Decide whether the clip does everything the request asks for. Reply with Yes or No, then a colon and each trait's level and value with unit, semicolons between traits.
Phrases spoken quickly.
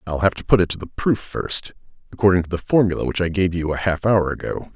Yes: fast, 265 wpm